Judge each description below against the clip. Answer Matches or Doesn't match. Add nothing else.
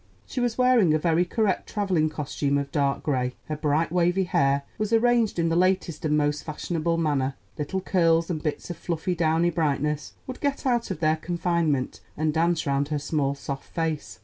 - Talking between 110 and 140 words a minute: Doesn't match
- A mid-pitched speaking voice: Matches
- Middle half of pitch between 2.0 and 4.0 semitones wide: Matches